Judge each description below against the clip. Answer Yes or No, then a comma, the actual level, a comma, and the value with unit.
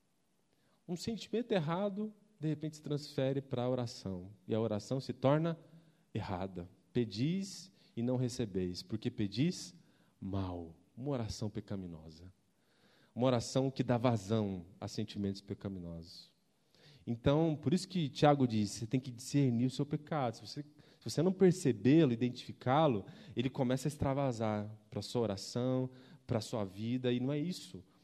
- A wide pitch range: Yes, wide, 6.0 semitones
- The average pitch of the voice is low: Yes, low, 125 Hz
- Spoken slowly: No, average, 150 wpm